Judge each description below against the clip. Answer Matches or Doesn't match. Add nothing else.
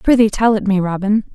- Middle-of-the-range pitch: Doesn't match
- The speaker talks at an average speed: Doesn't match